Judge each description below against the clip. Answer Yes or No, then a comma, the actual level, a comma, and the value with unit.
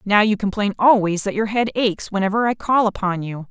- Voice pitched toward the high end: Yes, high, 205 Hz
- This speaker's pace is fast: Yes, fast, 225 wpm